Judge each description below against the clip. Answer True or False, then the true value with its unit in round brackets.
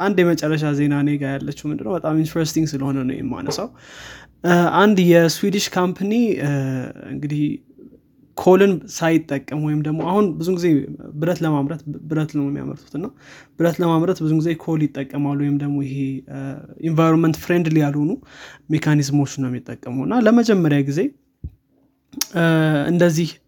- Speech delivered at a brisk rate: True (120 wpm)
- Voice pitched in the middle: True (155 Hz)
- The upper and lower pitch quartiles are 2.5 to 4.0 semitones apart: True (2.9 semitones)